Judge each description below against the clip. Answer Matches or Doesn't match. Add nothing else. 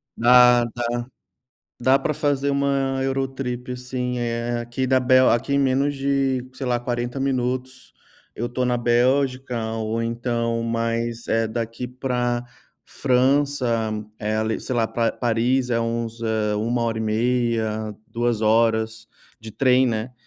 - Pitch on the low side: Matches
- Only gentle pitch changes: Matches